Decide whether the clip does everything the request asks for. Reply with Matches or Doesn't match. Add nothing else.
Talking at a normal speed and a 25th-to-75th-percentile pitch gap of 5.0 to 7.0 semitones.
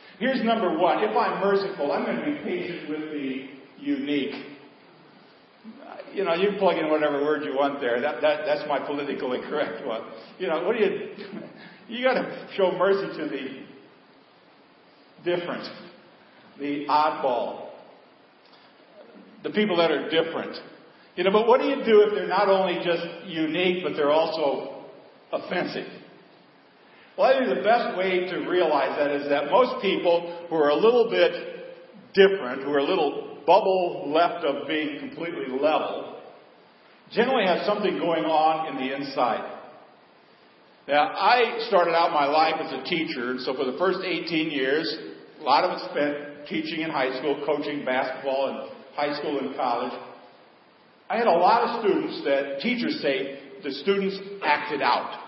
Matches